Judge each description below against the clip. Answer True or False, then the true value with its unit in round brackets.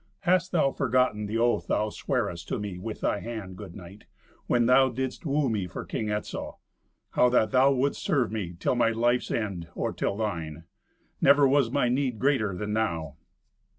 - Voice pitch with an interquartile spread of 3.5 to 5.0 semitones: True (4.2 semitones)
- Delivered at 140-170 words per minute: False (180 wpm)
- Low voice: True (115 Hz)